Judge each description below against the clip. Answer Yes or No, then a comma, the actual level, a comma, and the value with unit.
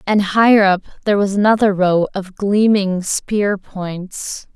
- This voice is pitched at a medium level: No, high, 200 Hz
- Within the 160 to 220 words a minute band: No, average, 145 wpm